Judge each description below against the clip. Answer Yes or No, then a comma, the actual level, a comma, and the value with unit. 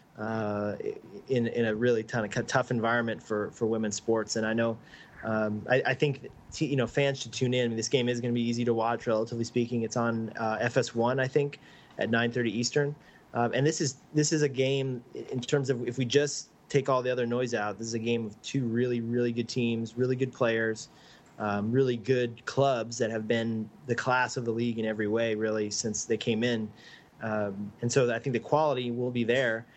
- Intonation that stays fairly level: Yes, narrow, 2.1 semitones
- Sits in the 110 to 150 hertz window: Yes, low, 120 Hz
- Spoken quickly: Yes, fast, 225 wpm